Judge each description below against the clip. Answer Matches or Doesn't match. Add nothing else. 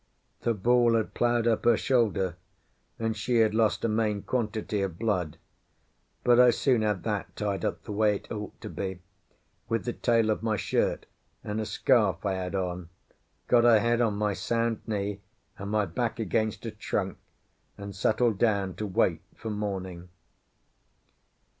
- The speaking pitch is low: Matches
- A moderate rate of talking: Matches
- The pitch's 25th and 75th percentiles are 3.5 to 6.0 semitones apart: Doesn't match